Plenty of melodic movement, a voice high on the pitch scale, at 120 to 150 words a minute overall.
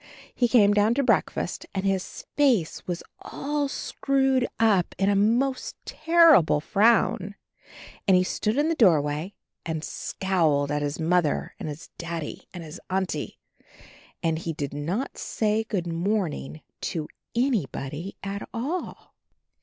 Yes: wide, 6.4 semitones; high, 195 Hz; average, 140 wpm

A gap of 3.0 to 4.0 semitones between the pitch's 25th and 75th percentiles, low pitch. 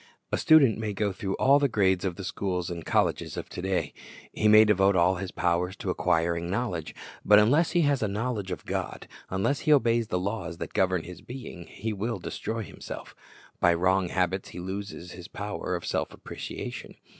Yes: average, 3.7 semitones; very low, 95 Hz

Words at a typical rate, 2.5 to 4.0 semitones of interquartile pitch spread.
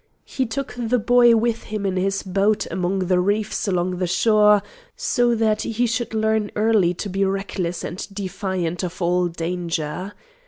Yes: average, 165 wpm; average, 3.4 semitones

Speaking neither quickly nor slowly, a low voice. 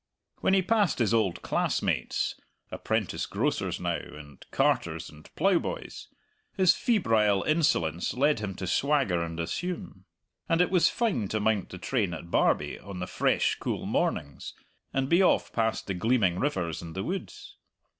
Yes: average, 155 wpm; low, 110 Hz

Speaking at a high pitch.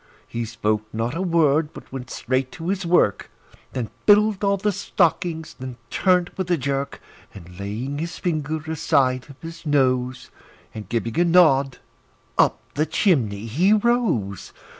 No: medium, 145 Hz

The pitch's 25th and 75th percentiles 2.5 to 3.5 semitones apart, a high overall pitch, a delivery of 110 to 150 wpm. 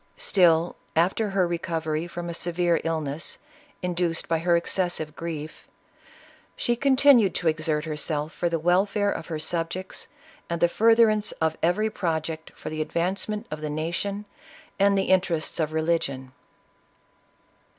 No: average, 3.2 semitones; medium, 170 Hz; average, 145 wpm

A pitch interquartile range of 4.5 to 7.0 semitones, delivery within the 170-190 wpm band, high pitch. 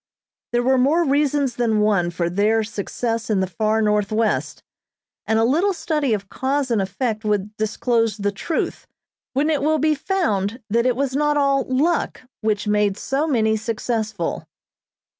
No: average, 4.8 semitones; average, 160 wpm; high, 230 Hz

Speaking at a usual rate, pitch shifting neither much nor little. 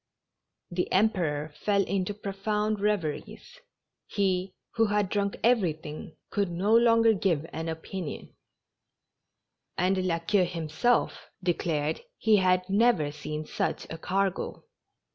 No: slow, 125 wpm; average, 4.1 semitones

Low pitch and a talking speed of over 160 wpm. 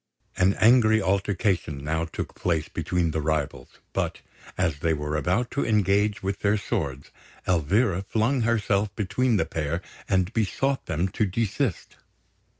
No: very low, 95 Hz; average, 145 wpm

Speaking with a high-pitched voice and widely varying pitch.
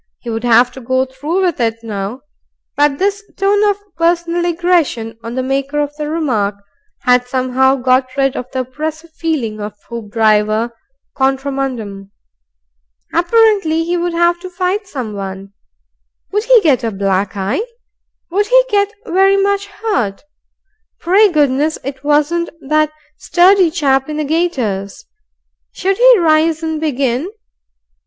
Yes: very high, 290 Hz; wide, 6.1 semitones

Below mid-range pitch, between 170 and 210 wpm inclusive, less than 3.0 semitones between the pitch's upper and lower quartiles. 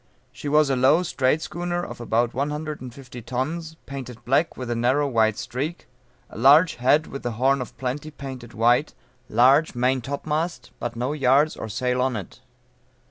No: low, 130 Hz; average, 180 wpm; average, 3.5 semitones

